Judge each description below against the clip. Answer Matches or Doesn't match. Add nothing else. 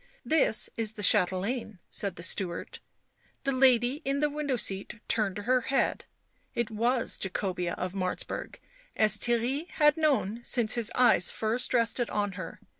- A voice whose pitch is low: Doesn't match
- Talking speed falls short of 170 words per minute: Matches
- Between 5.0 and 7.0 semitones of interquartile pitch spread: Doesn't match